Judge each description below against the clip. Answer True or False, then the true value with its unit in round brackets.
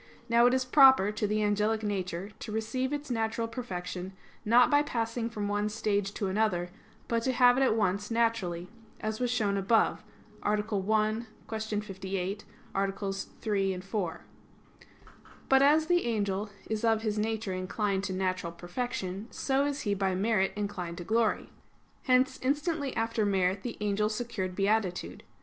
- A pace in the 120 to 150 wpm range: False (160 wpm)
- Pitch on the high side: True (215 Hz)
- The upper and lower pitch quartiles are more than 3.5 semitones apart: False (3.2 semitones)